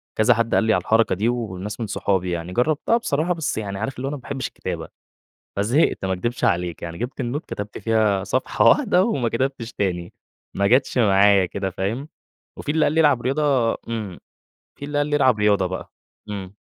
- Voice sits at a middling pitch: No, low, 115 Hz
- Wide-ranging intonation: Yes, wide, 5.7 semitones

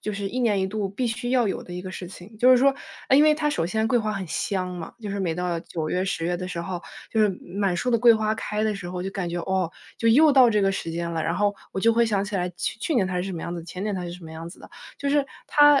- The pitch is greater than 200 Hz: No, high, 195 Hz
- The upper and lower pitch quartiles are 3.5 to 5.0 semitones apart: Yes, average, 4.3 semitones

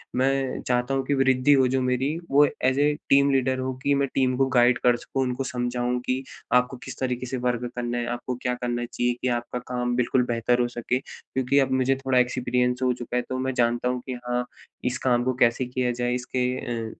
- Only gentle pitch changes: Yes, narrow, 1.2 semitones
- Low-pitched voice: Yes, low, 125 Hz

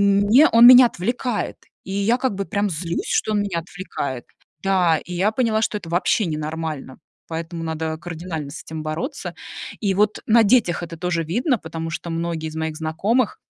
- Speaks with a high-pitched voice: No, medium, 180 Hz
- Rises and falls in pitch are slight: No, average, 4.8 semitones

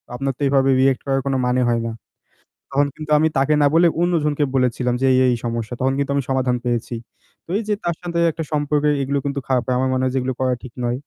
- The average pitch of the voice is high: No, low, 135 Hz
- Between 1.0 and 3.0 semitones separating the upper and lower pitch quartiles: Yes, narrow, 2.5 semitones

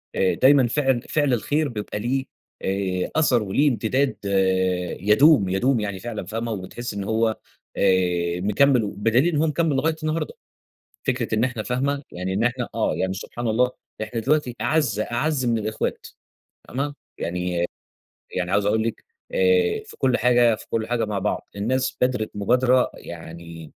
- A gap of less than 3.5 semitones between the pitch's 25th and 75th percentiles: No, average, 5.0 semitones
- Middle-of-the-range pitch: No, low, 115 Hz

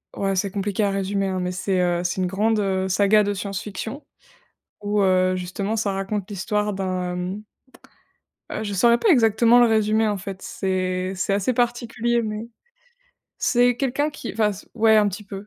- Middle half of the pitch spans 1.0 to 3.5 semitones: Yes, average, 2.7 semitones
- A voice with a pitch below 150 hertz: No, high, 205 Hz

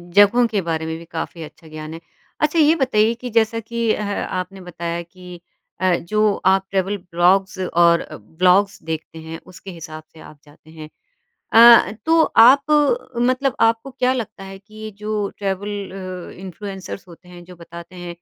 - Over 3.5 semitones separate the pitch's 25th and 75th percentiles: Yes, average, 4.1 semitones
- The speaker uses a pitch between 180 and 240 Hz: Yes, high, 190 Hz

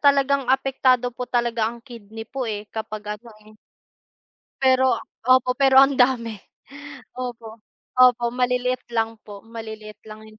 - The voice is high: Yes, high, 240 Hz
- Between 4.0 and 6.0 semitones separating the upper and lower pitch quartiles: No, narrow, 2.6 semitones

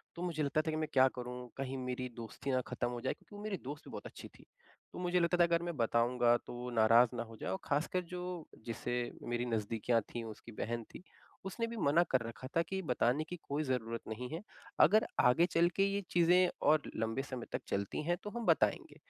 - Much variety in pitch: Yes, wide, 6.3 semitones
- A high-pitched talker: No, low, 135 Hz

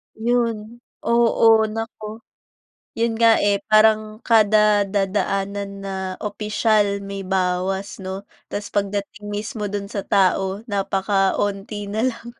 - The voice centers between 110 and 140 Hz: No, high, 205 Hz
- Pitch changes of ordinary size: No, narrow, 1.8 semitones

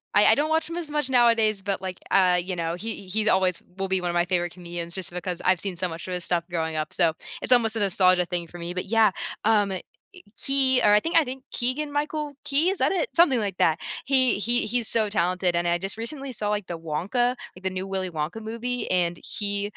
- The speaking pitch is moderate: No, high, 195 Hz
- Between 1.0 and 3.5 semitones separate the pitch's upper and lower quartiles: No, wide, 5.4 semitones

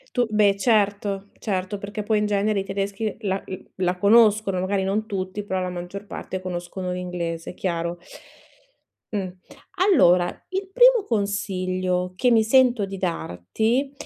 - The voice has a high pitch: Yes, high, 195 Hz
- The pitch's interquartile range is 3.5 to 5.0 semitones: No, average, 2.7 semitones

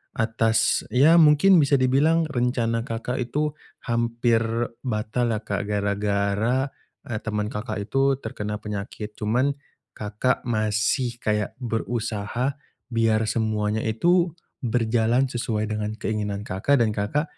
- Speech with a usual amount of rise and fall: Yes, average, 3.2 semitones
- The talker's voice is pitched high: No, low, 115 Hz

